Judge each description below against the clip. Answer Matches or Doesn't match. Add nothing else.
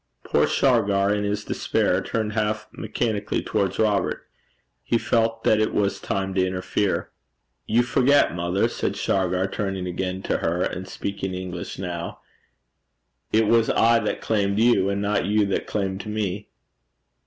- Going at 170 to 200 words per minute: Doesn't match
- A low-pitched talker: Matches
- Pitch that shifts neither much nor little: Doesn't match